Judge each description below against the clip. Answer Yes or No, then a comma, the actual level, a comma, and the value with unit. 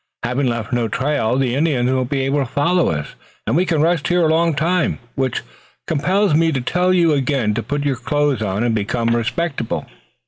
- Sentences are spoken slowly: No, fast, 205 wpm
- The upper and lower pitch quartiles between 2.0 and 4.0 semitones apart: No, average, 5.2 semitones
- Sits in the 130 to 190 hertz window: Yes, medium, 140 Hz